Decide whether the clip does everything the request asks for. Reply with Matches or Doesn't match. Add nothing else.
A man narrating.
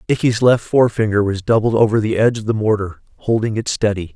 Matches